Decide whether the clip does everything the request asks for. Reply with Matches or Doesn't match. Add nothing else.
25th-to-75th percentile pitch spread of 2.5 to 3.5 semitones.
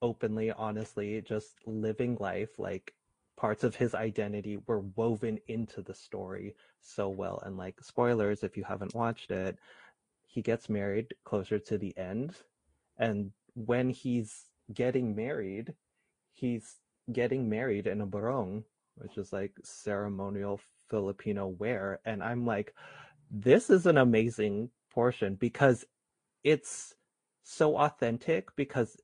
Matches